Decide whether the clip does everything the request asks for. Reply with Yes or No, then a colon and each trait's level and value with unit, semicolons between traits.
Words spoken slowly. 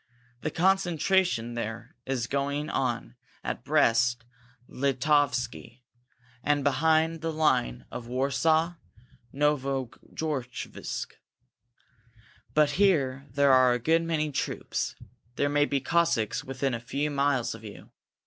Yes: slow, 115 wpm